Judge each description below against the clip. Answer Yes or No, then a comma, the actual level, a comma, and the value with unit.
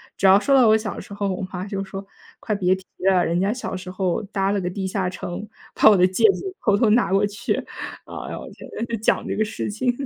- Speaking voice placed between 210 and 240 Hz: No, high, 200 Hz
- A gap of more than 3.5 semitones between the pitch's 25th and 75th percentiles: No, narrow, 2.4 semitones